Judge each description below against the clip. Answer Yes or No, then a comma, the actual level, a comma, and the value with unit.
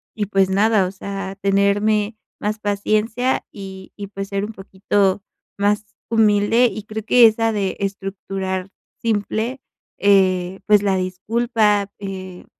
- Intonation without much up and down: Yes, narrow, 1.8 semitones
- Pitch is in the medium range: No, high, 200 Hz